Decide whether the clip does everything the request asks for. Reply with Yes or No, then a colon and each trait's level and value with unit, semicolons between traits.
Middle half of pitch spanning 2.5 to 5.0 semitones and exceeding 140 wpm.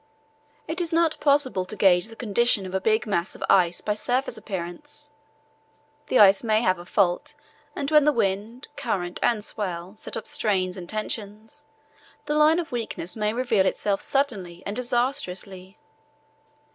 No: wide, 5.4 semitones; average, 160 wpm